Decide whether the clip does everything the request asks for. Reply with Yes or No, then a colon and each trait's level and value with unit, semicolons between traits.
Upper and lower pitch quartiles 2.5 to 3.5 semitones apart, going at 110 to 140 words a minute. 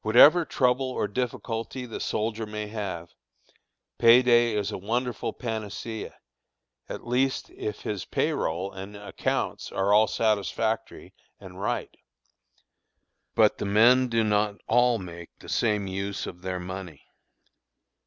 Yes: average, 3.2 semitones; slow, 135 wpm